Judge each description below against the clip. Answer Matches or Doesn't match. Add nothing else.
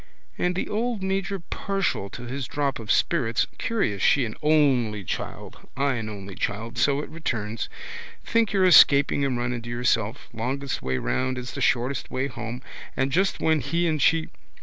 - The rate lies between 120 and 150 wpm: Doesn't match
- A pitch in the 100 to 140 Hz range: Matches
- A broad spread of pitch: Matches